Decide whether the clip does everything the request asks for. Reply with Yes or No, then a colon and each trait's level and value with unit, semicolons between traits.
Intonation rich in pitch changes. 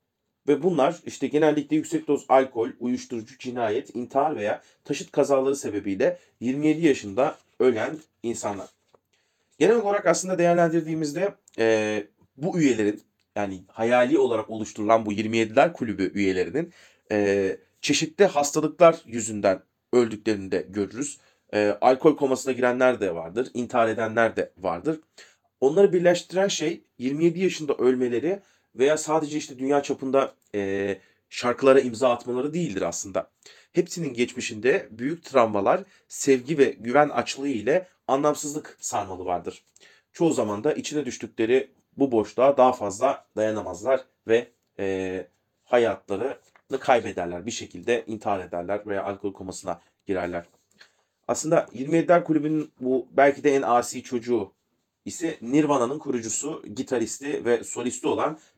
Yes: wide, 5.8 semitones